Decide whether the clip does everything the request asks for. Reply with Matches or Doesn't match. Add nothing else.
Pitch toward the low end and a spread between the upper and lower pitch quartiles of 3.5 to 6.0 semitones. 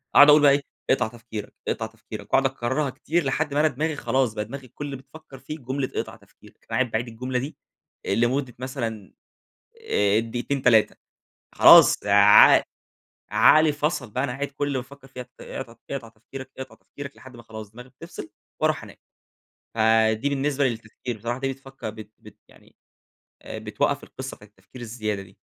Matches